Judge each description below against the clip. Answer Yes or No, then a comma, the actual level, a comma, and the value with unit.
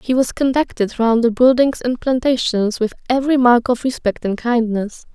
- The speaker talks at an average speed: Yes, average, 175 wpm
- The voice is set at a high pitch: Yes, high, 245 Hz